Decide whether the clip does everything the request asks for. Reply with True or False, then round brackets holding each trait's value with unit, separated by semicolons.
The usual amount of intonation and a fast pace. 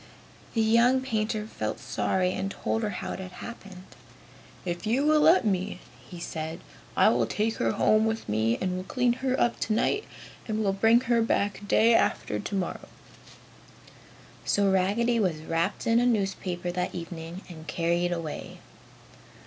False (4.5 semitones; 160 wpm)